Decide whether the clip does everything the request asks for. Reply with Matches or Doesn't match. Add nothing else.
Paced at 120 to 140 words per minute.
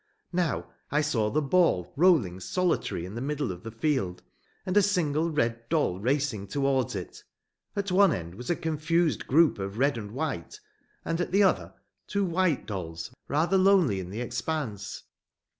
Doesn't match